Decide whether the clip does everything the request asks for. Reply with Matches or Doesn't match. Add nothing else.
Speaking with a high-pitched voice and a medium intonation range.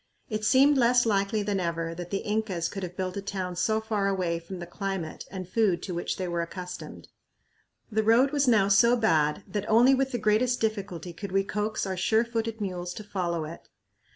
Matches